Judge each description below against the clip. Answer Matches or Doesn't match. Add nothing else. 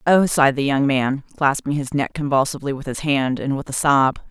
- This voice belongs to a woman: Matches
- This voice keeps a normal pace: Doesn't match